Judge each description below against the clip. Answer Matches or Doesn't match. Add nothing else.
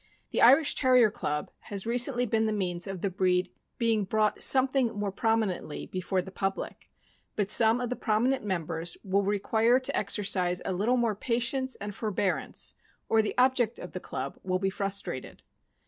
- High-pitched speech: Matches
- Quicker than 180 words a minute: Doesn't match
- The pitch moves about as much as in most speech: Matches